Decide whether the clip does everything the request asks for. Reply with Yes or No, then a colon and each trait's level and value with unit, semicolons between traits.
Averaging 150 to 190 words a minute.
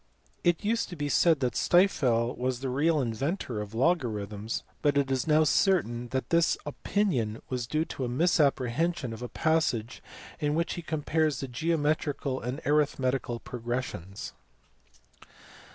No: average, 140 wpm